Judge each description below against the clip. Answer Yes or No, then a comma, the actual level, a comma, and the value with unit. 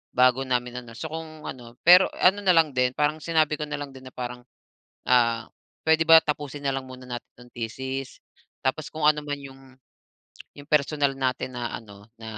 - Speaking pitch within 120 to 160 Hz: Yes, low, 135 Hz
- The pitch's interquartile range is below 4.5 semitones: Yes, average, 3.5 semitones